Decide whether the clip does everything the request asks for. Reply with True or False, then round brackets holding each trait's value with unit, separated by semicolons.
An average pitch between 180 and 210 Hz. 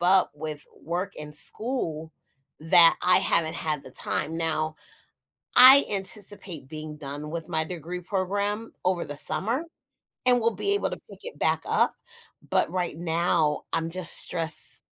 False (170 Hz)